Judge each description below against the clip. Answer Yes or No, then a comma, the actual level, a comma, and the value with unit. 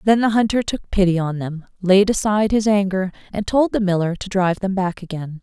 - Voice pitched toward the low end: No, high, 195 Hz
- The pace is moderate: No, fast, 220 wpm